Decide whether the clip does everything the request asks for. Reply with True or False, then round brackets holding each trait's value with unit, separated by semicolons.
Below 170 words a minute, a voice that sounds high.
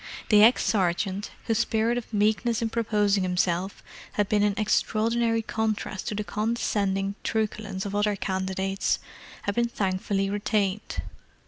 True (135 wpm; 210 Hz)